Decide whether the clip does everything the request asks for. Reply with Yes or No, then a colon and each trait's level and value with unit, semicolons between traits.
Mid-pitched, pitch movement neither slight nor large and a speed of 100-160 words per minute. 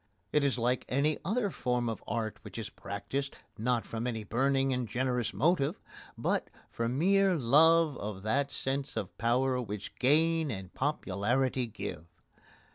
No: low, 125 Hz; average, 3.9 semitones; average, 150 wpm